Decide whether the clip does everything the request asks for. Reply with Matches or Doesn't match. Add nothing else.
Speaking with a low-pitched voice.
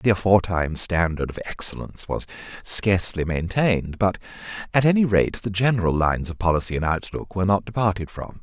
Matches